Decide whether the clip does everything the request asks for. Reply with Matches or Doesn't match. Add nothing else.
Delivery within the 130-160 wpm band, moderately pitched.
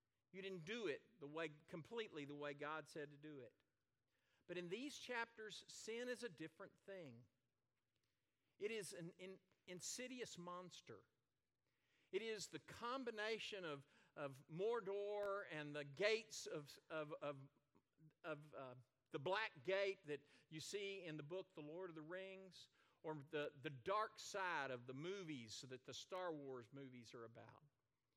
Matches